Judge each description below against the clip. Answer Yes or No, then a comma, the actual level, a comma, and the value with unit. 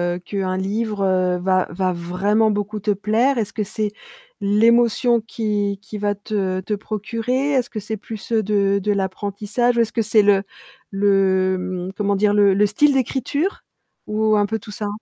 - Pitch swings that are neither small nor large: No, narrow, 2.2 semitones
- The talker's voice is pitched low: No, high, 205 Hz